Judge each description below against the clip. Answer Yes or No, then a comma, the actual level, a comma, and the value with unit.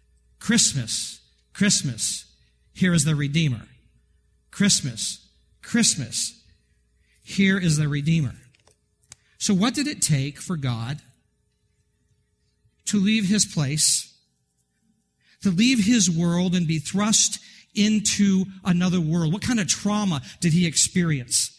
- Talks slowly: Yes, slow, 110 wpm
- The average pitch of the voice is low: No, medium, 150 Hz